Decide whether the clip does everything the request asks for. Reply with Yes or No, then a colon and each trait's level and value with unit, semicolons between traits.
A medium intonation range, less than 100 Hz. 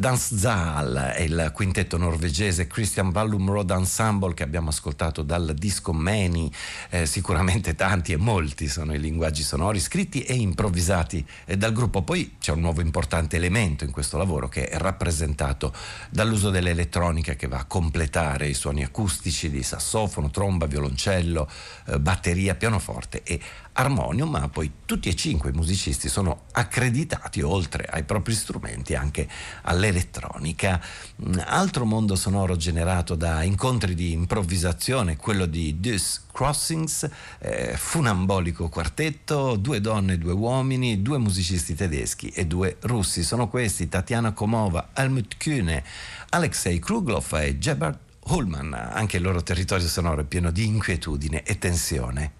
Yes: average, 4.2 semitones; very low, 90 Hz